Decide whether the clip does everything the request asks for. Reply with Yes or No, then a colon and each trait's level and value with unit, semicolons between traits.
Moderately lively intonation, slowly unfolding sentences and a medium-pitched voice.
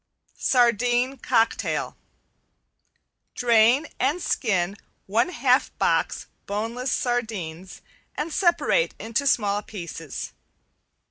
No: average, 4.0 semitones; slow, 80 wpm; high, 235 Hz